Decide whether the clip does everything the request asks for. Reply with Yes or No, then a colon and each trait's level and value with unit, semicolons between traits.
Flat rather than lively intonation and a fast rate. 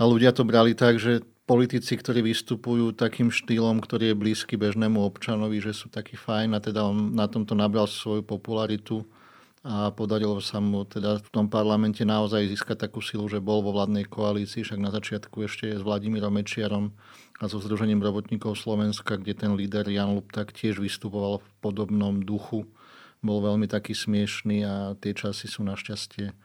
Yes: narrow, 1.2 semitones; fast, 175 wpm